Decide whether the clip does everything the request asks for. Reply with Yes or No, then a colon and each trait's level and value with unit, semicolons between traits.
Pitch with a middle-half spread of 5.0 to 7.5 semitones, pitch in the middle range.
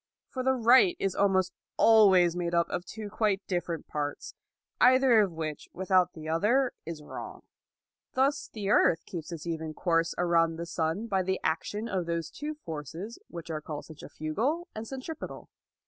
Yes: average, 5.3 semitones; medium, 180 Hz